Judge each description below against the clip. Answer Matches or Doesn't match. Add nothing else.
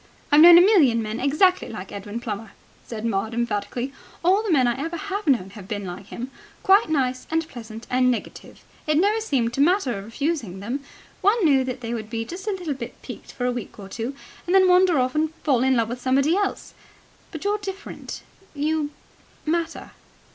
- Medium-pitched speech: Doesn't match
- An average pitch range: Doesn't match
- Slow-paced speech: Doesn't match